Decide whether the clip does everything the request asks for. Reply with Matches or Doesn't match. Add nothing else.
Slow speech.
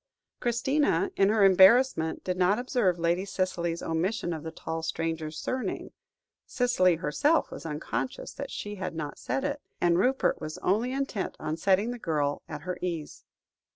Doesn't match